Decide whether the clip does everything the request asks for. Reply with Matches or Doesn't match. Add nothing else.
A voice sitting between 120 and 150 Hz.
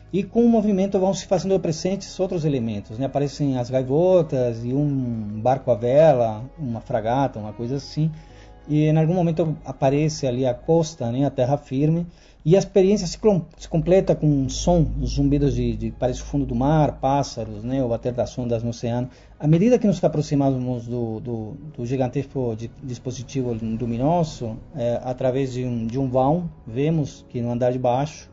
Matches